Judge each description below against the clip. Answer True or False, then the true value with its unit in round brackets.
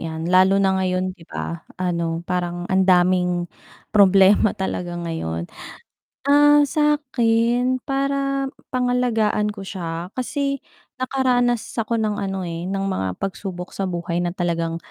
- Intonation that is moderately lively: False (5.9 semitones)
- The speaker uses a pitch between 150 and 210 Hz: True (190 Hz)